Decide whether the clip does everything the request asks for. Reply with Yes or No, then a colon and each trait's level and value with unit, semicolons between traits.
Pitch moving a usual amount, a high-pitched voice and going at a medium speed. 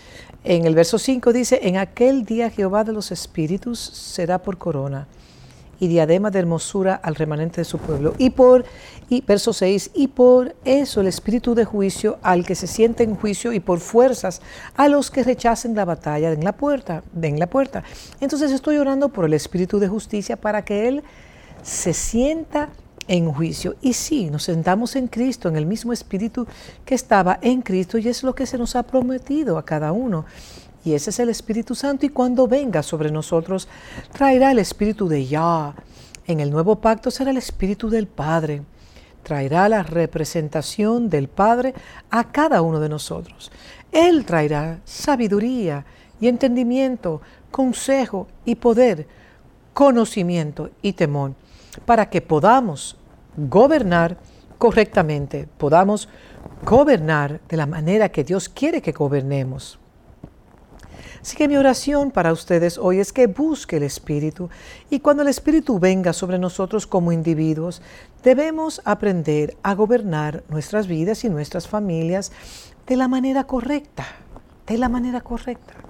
No: wide, 7.1 semitones; high, 205 Hz; average, 155 wpm